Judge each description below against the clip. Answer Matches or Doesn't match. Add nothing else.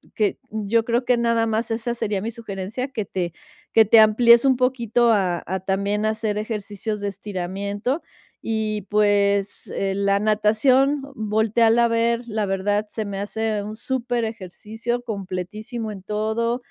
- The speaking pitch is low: Doesn't match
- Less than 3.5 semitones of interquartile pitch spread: Matches